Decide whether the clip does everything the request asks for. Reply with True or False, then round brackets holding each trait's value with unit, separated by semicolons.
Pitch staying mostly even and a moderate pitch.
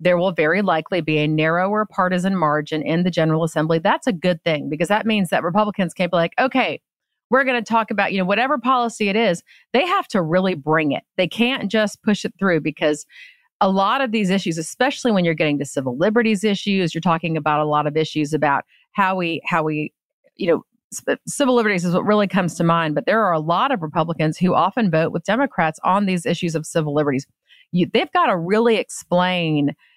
False (5.1 semitones; 180 Hz)